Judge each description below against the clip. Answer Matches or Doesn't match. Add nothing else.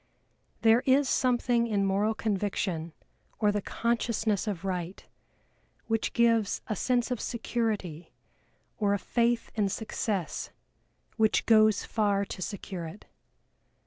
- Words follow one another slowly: Matches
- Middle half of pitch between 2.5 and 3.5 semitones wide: Matches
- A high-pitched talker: Matches